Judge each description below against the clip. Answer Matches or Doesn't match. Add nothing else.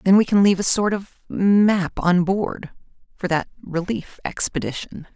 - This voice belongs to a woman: Matches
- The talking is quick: Doesn't match